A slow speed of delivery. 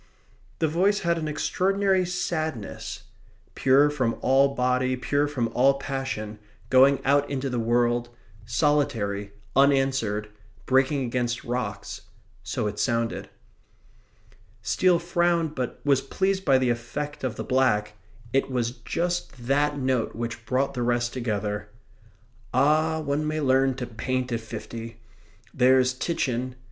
Yes: slow, 130 wpm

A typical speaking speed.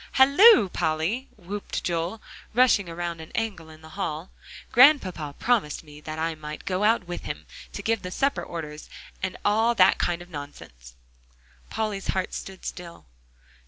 Yes: average, 160 wpm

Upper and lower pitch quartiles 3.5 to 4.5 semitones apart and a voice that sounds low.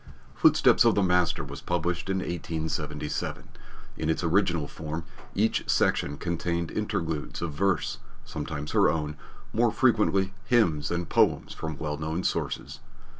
No: average, 2.7 semitones; very low, 85 Hz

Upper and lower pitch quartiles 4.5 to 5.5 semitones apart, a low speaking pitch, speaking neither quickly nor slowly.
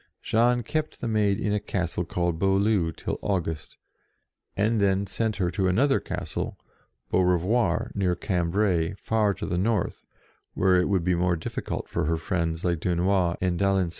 No: average, 2.9 semitones; very low, 95 Hz; average, 165 wpm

